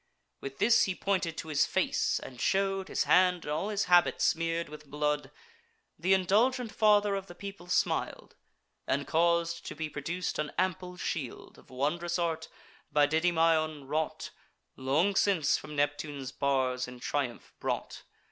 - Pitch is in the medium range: Yes, medium, 165 Hz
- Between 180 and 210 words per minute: No, average, 155 wpm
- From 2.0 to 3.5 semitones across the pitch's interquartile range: No, average, 4.1 semitones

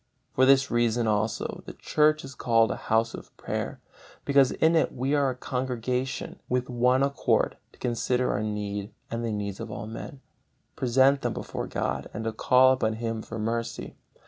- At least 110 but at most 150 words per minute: No, average, 180 wpm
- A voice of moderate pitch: No, low, 120 Hz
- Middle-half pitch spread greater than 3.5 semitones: No, average, 2.8 semitones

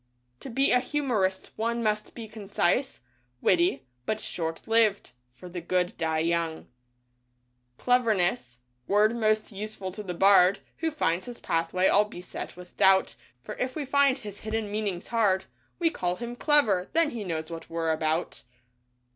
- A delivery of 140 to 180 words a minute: Yes, average, 165 wpm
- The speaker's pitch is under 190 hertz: No, high, 200 Hz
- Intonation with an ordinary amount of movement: Yes, average, 4.8 semitones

